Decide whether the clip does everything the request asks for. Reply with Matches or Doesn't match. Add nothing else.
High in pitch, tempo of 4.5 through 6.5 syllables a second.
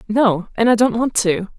Matches